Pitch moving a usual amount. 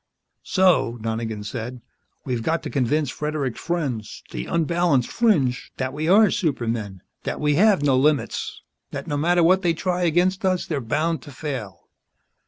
No: wide, 6.0 semitones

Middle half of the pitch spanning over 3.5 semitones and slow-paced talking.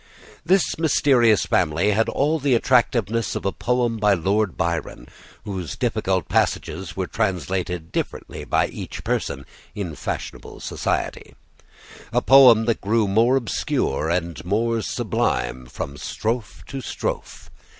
Yes: average, 5.2 semitones; slow, 130 wpm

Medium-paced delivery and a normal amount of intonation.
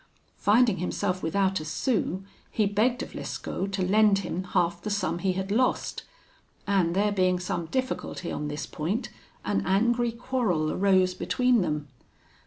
Yes: average, 155 wpm; average, 3.2 semitones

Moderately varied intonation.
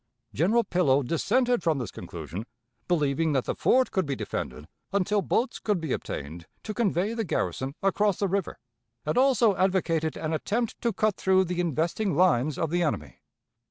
No: wide, 5.7 semitones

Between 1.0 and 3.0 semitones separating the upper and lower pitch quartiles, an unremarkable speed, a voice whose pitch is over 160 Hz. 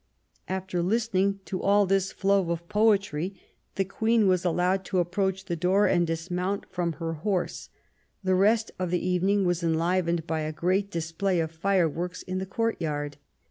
Yes: narrow, 2.5 semitones; average, 165 wpm; medium, 185 Hz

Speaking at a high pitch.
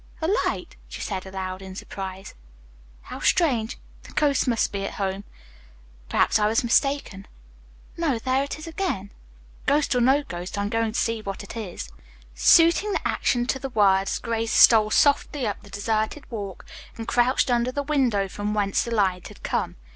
Yes: high, 225 Hz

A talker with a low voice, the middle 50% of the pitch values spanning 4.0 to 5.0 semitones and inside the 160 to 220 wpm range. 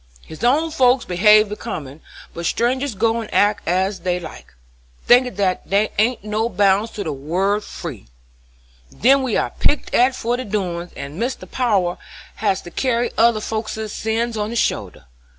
No: high, 215 Hz; average, 4.3 semitones; average, 170 wpm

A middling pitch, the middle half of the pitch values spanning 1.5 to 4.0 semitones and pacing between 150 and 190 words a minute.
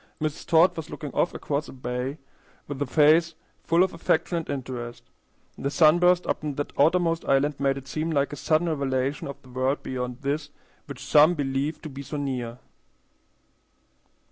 Yes: medium, 145 Hz; average, 2.9 semitones; average, 170 wpm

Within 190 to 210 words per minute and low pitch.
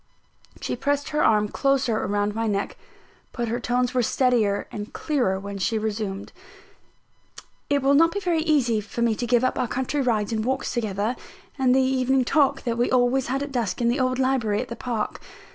No: average, 200 wpm; high, 245 Hz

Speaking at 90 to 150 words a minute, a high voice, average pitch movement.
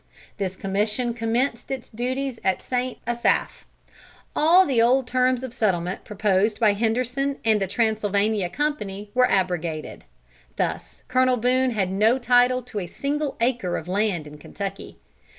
Yes: average, 145 wpm; high, 230 Hz; average, 4.4 semitones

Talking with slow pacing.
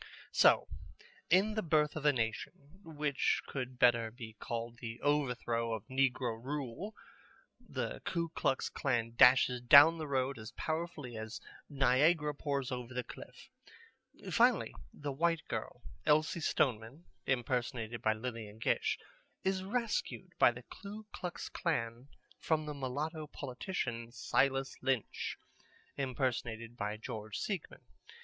Yes: slow, 130 wpm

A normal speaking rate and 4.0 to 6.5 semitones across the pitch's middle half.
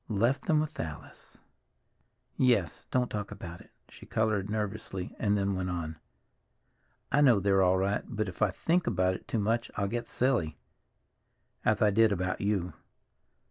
No: average, 160 wpm; average, 3.5 semitones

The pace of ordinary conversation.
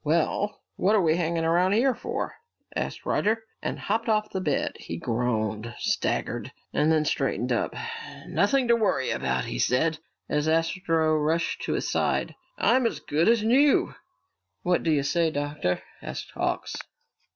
Yes: average, 160 wpm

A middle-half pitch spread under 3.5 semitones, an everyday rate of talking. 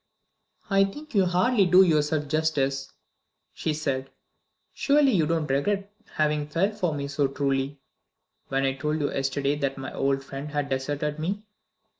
No: average, 4.6 semitones; average, 155 wpm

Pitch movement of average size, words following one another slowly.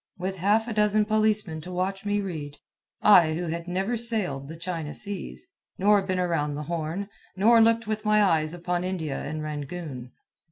No: average, 4.8 semitones; average, 175 wpm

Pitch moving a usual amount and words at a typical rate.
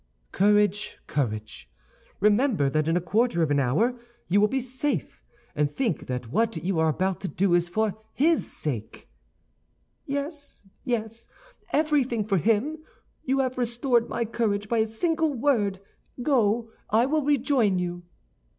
No: wide, 6.4 semitones; average, 150 wpm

